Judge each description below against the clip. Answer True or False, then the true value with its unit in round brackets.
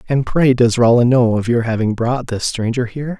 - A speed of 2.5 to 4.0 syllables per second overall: False (5.3 syllables/s)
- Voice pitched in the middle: False (120 Hz)